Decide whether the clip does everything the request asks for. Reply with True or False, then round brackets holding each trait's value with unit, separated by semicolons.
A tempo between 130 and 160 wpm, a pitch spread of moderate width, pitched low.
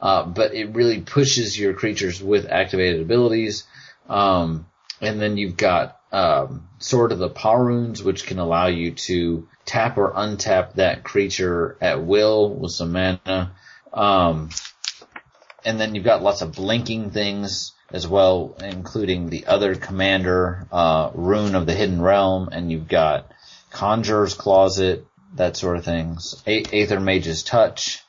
True (150 wpm; 3.0 semitones; 95 Hz)